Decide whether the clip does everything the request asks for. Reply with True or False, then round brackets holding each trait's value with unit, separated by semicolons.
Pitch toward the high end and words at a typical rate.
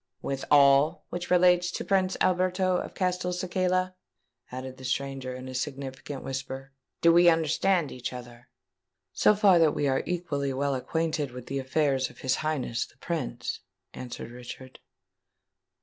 False (145 Hz; 150 wpm)